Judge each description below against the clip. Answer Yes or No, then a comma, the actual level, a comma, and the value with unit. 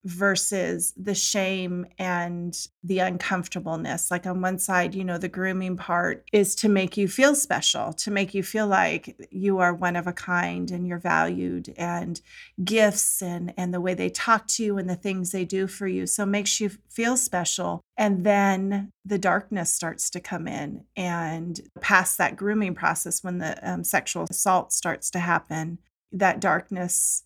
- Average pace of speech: Yes, average, 180 wpm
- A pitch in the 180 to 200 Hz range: Yes, medium, 185 Hz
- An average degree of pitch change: No, narrow, 2.3 semitones